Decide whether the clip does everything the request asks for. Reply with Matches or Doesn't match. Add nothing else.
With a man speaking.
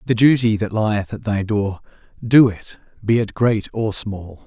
Matches